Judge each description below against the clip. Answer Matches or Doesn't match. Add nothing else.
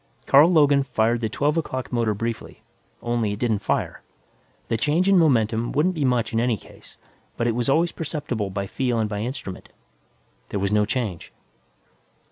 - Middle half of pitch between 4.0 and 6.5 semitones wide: Matches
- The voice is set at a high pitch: Doesn't match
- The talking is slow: Doesn't match